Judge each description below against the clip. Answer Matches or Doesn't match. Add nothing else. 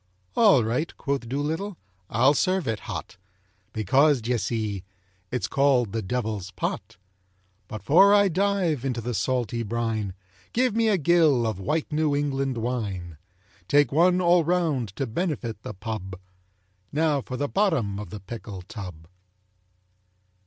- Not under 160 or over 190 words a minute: Doesn't match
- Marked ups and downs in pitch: Matches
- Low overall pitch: Matches